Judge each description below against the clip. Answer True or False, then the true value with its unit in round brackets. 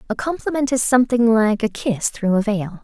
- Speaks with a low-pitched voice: False (225 Hz)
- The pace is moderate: False (210 wpm)